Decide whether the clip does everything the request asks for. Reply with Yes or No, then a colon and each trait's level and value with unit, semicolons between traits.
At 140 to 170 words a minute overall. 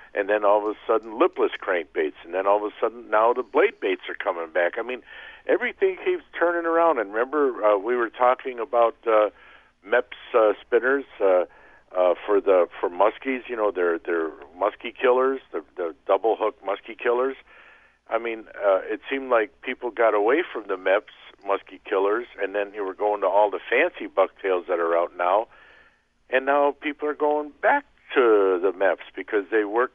No: average, 190 wpm